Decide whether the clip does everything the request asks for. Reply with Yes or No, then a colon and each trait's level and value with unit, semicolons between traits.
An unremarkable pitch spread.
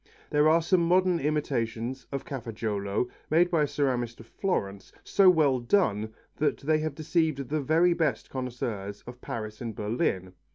No: wide, 5.7 semitones